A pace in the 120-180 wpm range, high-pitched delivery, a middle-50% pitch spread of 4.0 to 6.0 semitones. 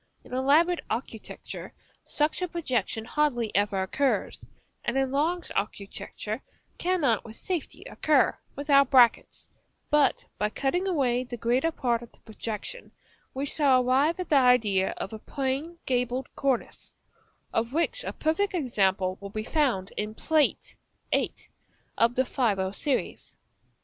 Yes: average, 140 wpm; very high, 260 Hz; average, 5.1 semitones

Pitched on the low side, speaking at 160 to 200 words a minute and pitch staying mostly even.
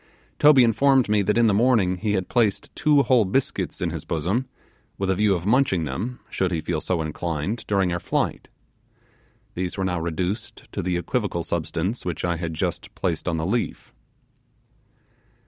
No: very low, 95 Hz; average, 180 wpm; average, 4.9 semitones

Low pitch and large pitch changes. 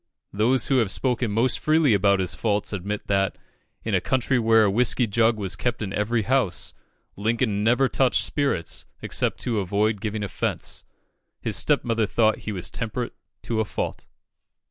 No: low, 110 Hz; average, 3.1 semitones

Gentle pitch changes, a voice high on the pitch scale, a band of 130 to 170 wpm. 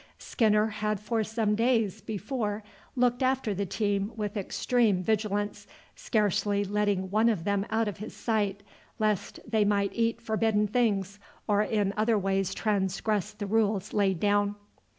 Yes: narrow, 1.7 semitones; high, 210 Hz; average, 150 wpm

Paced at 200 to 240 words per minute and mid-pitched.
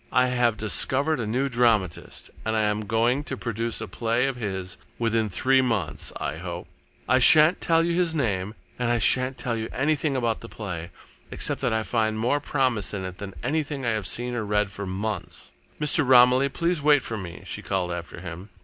No: fast, 205 wpm; low, 115 Hz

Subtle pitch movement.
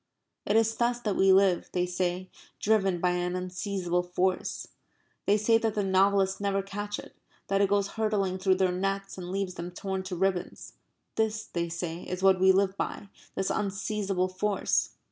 Yes: narrow, 1.7 semitones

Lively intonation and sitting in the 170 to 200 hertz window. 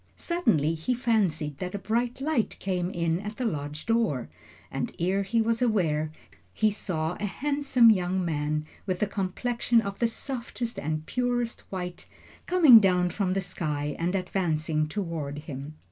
Yes: wide, 6.4 semitones; high, 190 Hz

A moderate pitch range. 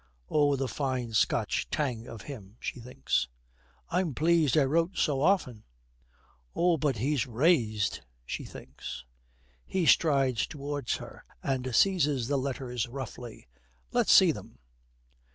Yes: average, 4.0 semitones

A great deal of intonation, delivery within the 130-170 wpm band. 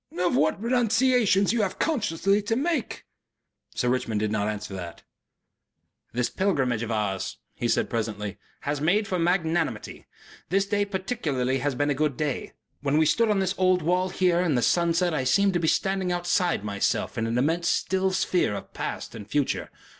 No: wide, 7.3 semitones; average, 180 wpm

